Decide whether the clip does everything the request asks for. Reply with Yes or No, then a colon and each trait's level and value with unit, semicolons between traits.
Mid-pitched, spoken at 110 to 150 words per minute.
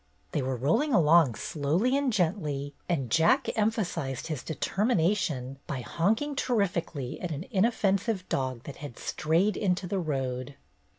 Yes: medium, 170 Hz; slow, 135 wpm